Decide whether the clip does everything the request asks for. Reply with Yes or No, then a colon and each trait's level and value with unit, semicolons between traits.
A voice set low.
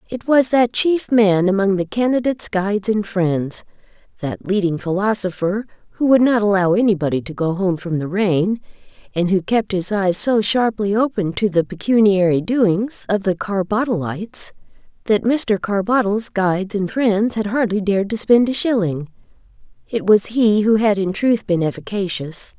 No: high, 205 Hz